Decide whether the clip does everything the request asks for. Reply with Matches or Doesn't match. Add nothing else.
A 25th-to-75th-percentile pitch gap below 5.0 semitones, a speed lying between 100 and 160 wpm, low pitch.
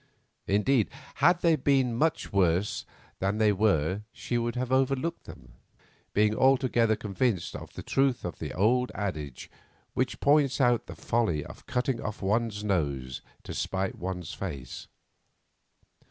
Doesn't match